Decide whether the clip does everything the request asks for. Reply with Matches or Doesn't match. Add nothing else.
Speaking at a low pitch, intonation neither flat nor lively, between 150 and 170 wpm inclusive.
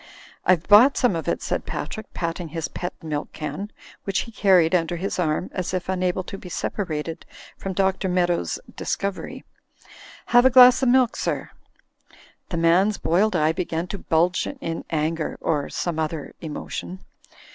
Doesn't match